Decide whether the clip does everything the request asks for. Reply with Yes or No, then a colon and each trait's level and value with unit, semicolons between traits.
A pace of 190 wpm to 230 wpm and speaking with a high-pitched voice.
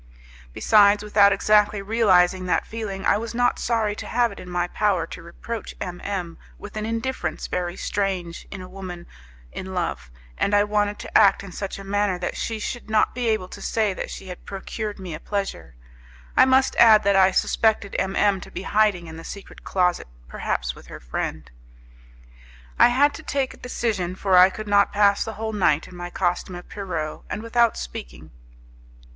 Yes: average, 195 wpm; high, 200 Hz